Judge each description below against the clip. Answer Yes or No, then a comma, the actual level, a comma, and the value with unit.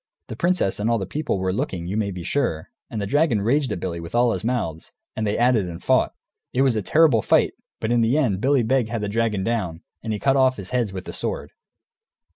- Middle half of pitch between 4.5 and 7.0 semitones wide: Yes, average, 4.9 semitones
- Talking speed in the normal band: No, fast, 255 wpm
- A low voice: Yes, low, 110 Hz